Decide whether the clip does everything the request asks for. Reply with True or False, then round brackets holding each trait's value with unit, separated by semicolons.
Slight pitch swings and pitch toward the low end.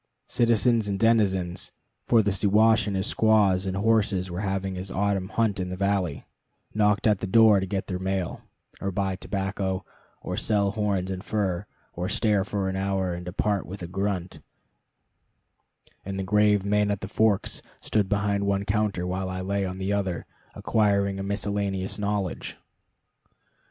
True (1.6 semitones; 100 Hz)